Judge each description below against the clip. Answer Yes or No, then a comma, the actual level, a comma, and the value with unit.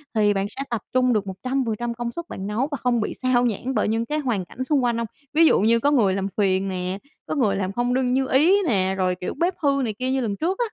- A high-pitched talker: Yes, high, 235 Hz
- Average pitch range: Yes, average, 4.7 semitones